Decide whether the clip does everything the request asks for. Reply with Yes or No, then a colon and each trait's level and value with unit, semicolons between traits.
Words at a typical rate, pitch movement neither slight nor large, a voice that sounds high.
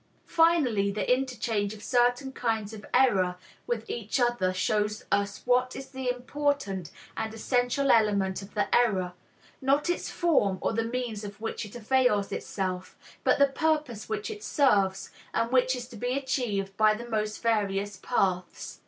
Yes: average, 160 wpm; average, 4.0 semitones; high, 230 Hz